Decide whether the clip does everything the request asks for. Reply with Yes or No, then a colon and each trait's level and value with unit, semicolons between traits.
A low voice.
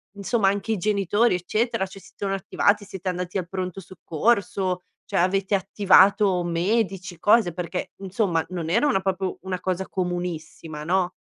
No: high, 190 Hz